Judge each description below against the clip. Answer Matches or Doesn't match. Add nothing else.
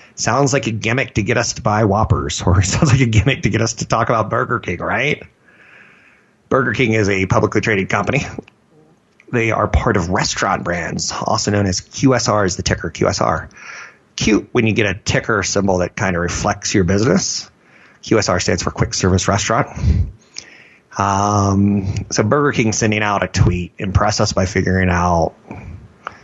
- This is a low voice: Matches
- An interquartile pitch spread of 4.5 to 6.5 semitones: Doesn't match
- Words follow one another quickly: Doesn't match